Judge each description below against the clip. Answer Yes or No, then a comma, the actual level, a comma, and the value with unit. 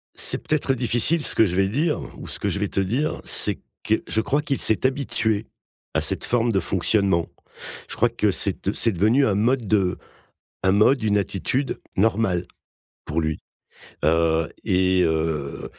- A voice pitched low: Yes, low, 105 Hz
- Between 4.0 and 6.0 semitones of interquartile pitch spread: Yes, average, 4.6 semitones